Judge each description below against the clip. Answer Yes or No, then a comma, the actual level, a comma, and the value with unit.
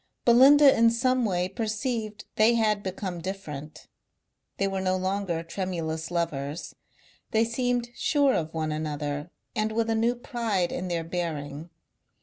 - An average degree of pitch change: No, wide, 5.7 semitones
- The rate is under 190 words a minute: Yes, average, 140 wpm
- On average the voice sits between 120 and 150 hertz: No, high, 195 Hz